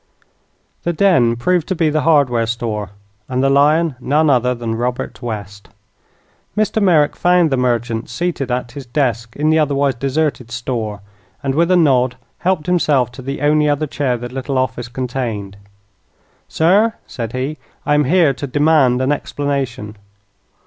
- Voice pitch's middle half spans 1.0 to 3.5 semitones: No, average, 4.0 semitones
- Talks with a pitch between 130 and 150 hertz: Yes, low, 135 Hz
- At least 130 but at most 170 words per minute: Yes, average, 160 wpm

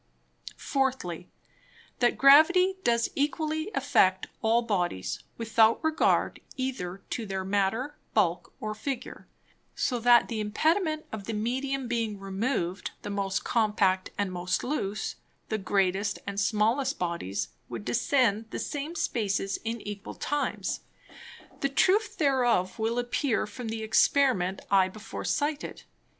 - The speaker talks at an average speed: No, slow, 130 wpm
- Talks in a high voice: Yes, high, 225 Hz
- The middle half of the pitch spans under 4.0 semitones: No, wide, 5.5 semitones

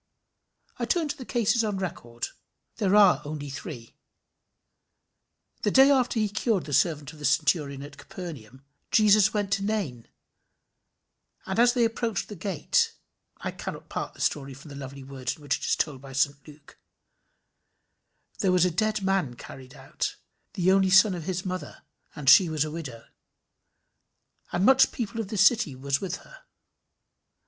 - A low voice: No, medium, 180 Hz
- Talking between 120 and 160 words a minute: No, average, 170 wpm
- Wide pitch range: Yes, wide, 6.8 semitones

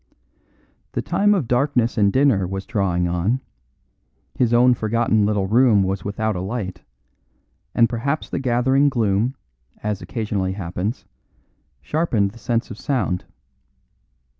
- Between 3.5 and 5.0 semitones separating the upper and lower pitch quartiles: Yes, average, 4.1 semitones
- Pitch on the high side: No, low, 110 Hz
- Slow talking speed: Yes, slow, 130 wpm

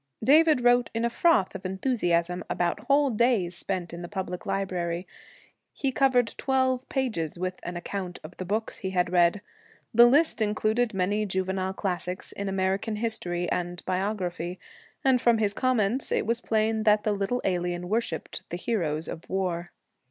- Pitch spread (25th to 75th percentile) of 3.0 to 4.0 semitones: No, average, 4.7 semitones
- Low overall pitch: No, high, 195 Hz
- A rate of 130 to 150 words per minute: No, average, 165 wpm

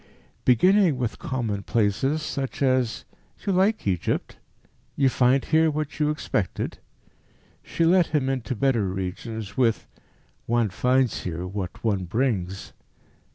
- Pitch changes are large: Yes, wide, 5.9 semitones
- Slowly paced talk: Yes, slow, 120 wpm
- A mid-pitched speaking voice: No, low, 125 Hz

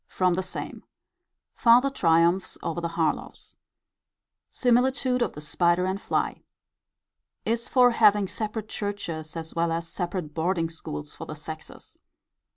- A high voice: No, medium, 180 Hz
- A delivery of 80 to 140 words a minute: Yes, slow, 135 wpm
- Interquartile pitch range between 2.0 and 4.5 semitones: No, average, 4.9 semitones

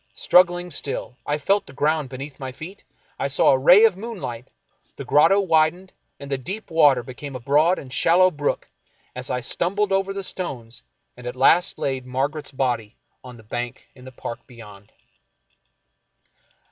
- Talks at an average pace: Yes, average, 175 wpm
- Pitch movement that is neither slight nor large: No, wide, 5.8 semitones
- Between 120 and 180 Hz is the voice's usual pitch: Yes, medium, 140 Hz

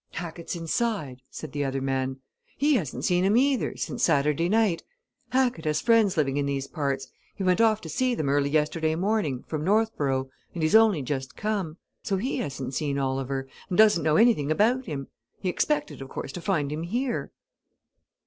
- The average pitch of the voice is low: No, medium, 160 Hz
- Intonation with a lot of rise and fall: Yes, wide, 7.3 semitones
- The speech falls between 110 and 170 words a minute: No, average, 185 wpm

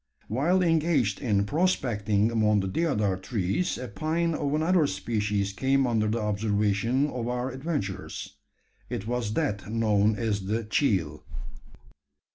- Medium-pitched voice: No, low, 115 Hz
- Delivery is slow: Yes, slow, 130 wpm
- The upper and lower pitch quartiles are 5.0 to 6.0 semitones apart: Yes, wide, 5.4 semitones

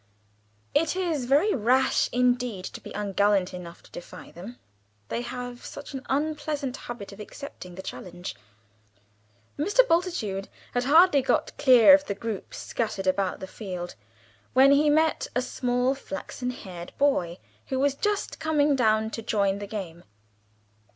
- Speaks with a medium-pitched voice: No, high, 245 Hz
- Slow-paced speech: No, average, 150 wpm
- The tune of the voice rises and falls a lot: Yes, wide, 6.3 semitones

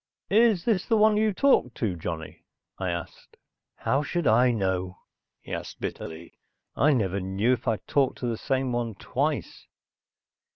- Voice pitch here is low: Yes, low, 120 Hz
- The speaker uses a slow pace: No, average, 160 wpm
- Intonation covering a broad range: Yes, wide, 8.4 semitones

